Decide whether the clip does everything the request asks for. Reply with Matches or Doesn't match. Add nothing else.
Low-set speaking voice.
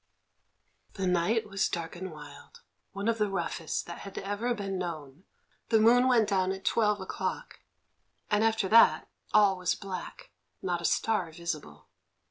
Doesn't match